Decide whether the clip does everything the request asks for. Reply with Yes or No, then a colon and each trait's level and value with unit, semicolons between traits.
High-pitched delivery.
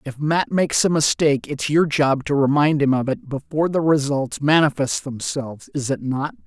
No: medium, 145 Hz